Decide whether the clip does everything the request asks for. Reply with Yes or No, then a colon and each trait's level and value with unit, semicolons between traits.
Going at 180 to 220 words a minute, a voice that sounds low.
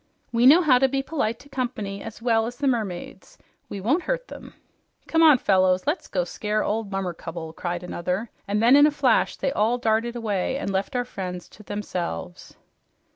No: average, 190 wpm; high, 225 Hz